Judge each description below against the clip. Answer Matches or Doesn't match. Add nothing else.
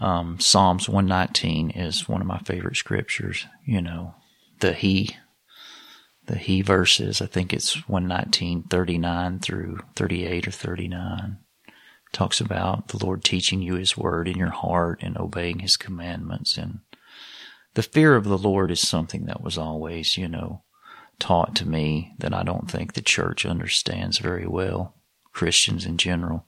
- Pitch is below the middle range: Matches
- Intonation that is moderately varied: Doesn't match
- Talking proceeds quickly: Doesn't match